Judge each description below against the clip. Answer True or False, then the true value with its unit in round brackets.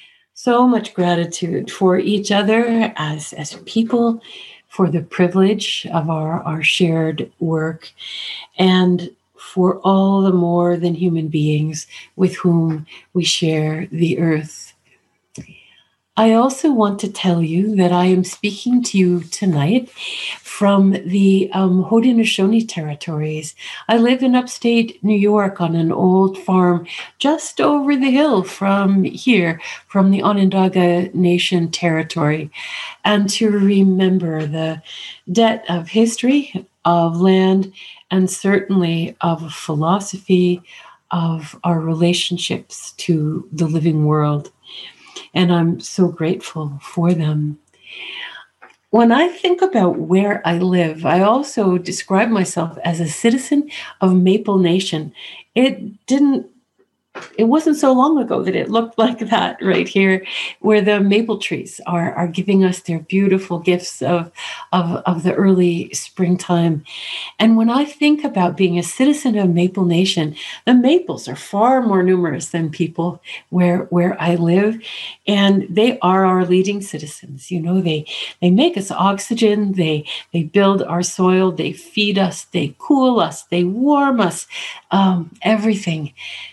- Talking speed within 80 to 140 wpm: True (135 wpm)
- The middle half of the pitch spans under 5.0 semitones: True (3.7 semitones)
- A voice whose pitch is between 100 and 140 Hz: False (185 Hz)